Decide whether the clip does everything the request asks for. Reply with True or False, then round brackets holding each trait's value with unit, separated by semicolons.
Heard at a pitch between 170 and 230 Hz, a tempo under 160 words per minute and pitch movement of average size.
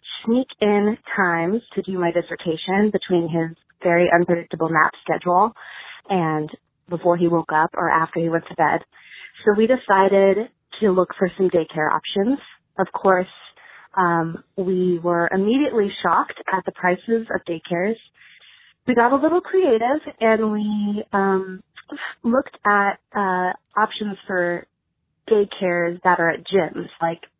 True (190 Hz; 140 wpm; 3.7 semitones)